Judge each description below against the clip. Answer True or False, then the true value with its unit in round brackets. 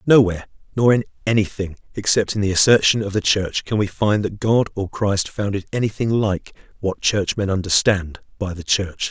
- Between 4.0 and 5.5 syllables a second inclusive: True (5.2 syllables/s)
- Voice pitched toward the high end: False (100 Hz)